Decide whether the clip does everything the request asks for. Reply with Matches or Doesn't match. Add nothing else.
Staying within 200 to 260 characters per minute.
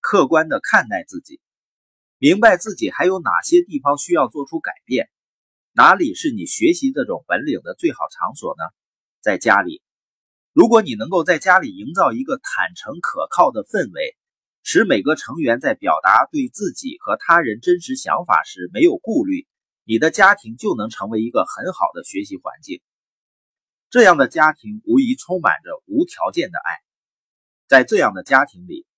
Matches